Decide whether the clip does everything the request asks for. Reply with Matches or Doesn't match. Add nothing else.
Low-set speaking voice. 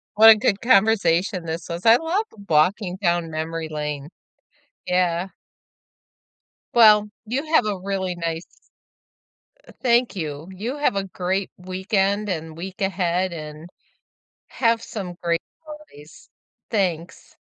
Doesn't match